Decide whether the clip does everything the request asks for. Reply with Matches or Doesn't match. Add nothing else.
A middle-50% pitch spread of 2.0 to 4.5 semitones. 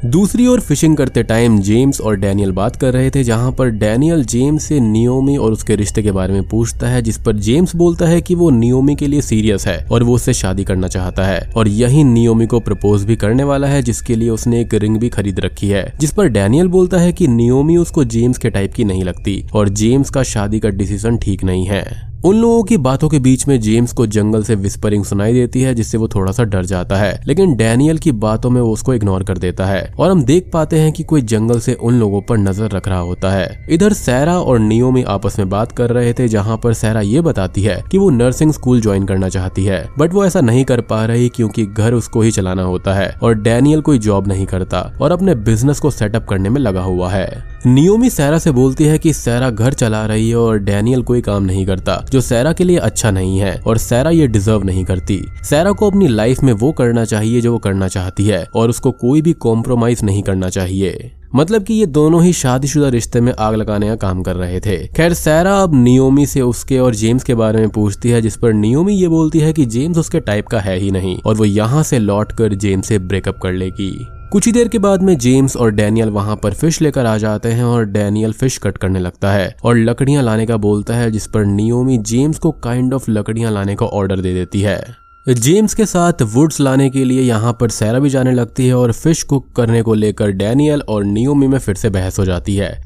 Doesn't match